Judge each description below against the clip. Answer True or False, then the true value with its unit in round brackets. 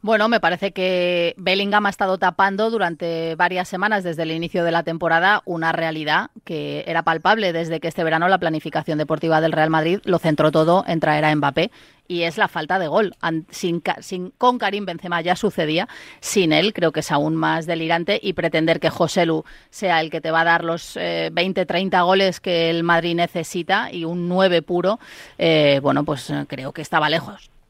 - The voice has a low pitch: False (170 Hz)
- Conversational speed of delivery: False (200 wpm)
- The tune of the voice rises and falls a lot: False (2.4 semitones)